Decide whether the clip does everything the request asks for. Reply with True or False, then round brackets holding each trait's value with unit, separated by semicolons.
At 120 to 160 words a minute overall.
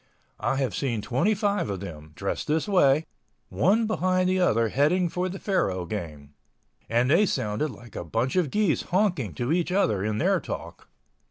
False (170 wpm)